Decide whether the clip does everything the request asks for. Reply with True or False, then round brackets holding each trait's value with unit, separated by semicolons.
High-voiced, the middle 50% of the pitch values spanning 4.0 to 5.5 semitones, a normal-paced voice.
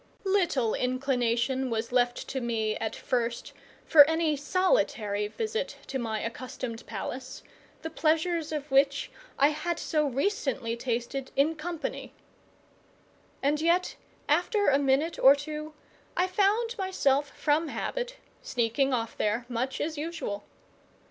False (275 Hz; 5.0 semitones; 130 wpm)